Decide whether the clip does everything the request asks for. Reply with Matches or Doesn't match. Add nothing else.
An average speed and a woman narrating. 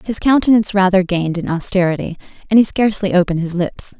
Matches